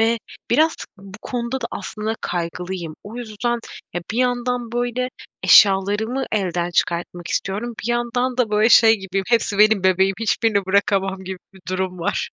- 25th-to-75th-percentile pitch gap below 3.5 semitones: No, average, 4.0 semitones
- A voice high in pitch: Yes, high, 210 Hz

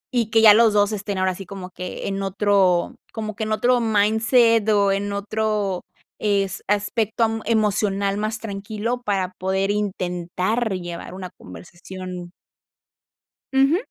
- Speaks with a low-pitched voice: No, high, 205 Hz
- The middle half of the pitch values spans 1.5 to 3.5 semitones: Yes, narrow, 2.6 semitones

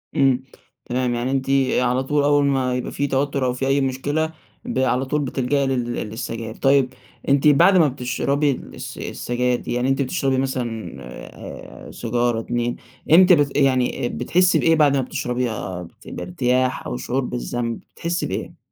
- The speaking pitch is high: No, low, 130 Hz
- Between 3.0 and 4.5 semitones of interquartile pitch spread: No, narrow, 2.4 semitones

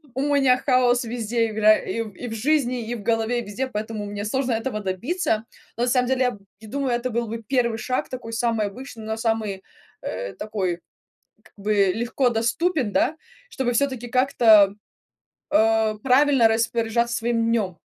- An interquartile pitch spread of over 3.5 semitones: No, average, 2.7 semitones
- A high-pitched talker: Yes, high, 230 Hz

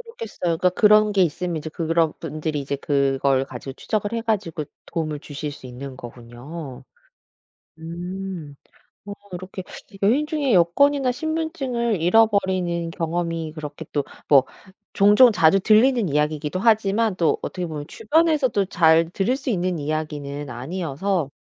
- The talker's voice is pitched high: No, medium, 170 Hz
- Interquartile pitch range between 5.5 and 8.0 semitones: Yes, wide, 5.9 semitones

